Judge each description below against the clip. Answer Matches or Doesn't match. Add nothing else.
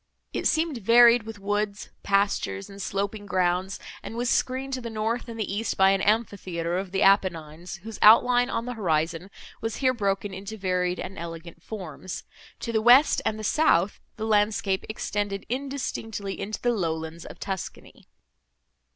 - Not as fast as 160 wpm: Doesn't match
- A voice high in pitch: Matches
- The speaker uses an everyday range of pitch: Matches